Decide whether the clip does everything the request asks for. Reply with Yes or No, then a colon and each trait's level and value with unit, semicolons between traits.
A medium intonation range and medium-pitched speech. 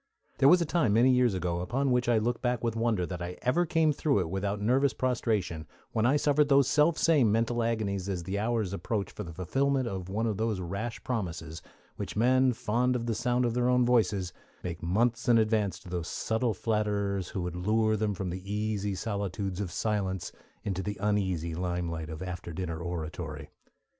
No: average, 4.9 semitones; low, 105 Hz